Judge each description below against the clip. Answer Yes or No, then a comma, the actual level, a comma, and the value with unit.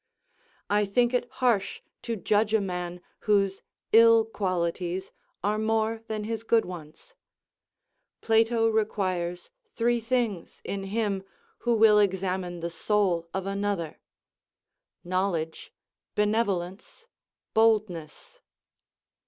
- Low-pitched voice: No, high, 205 Hz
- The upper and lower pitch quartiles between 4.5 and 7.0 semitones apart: No, average, 3.5 semitones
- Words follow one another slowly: Yes, slow, 105 wpm